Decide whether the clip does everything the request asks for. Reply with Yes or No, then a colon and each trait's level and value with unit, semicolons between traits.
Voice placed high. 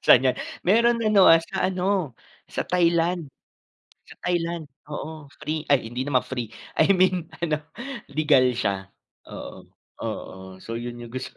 No: medium, 155 Hz